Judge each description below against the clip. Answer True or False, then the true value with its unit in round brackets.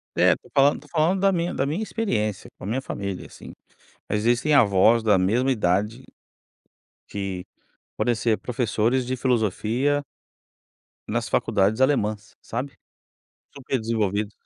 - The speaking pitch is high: False (115 Hz)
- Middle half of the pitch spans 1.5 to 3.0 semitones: False (4.3 semitones)